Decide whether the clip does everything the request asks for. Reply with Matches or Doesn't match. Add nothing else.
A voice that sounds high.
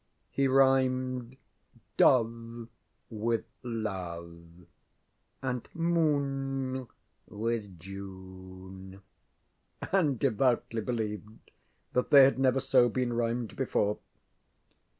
Doesn't match